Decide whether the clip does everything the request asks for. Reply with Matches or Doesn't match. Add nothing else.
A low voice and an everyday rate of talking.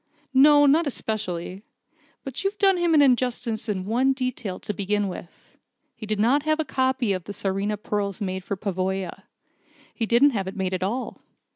Doesn't match